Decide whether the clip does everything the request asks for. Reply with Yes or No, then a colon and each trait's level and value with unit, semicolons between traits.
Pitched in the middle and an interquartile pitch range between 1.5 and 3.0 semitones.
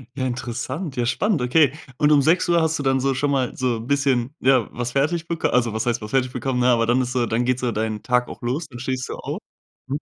No: low, 130 Hz; average, 2.7 semitones